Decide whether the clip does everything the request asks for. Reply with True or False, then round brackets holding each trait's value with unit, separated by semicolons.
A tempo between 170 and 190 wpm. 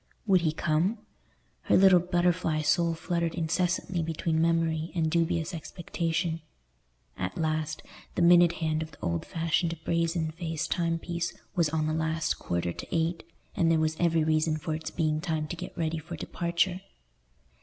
False (160 wpm)